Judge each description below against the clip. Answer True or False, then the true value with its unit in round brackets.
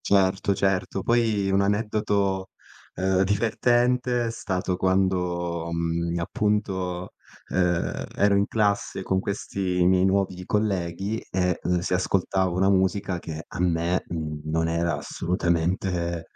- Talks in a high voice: False (95 Hz)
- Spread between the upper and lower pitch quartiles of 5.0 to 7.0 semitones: False (2.4 semitones)